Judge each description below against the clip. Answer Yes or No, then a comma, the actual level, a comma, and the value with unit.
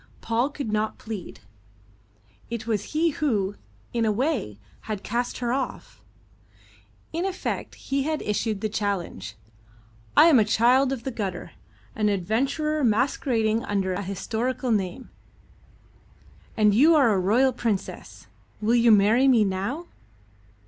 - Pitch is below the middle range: No, high, 230 Hz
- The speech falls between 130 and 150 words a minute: Yes, slow, 135 wpm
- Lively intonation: No, average, 4.3 semitones